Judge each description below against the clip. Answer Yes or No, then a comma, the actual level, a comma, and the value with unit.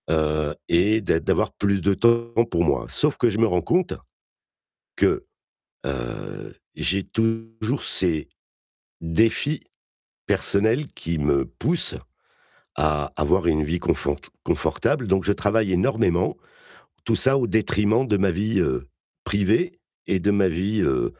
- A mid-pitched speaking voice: No, low, 100 Hz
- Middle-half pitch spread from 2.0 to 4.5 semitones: No, wide, 5.4 semitones